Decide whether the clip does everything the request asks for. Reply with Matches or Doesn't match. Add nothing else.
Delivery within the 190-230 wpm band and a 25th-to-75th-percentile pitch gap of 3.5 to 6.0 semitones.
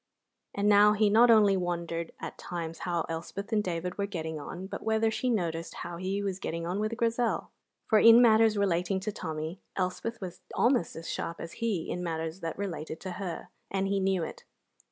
Matches